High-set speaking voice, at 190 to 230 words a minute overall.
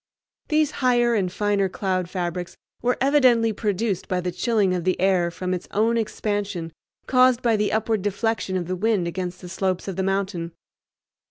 No: high, 195 Hz; average, 175 wpm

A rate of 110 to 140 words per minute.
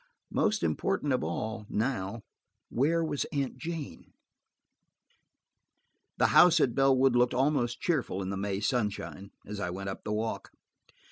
Yes: slow, 135 wpm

